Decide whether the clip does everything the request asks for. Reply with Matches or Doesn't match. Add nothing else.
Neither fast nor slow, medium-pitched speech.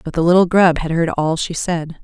Doesn't match